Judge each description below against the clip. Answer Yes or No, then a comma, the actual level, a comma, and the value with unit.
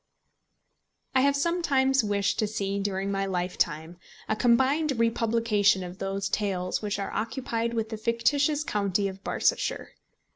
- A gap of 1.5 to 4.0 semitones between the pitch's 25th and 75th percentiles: Yes, average, 3.7 semitones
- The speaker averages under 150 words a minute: Yes, average, 140 wpm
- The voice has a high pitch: Yes, high, 215 Hz